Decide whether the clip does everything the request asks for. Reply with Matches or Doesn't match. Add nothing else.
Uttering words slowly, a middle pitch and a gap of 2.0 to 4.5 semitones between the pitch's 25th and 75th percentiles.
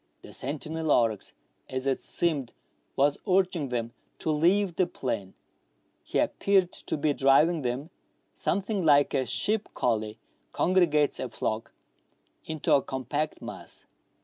Doesn't match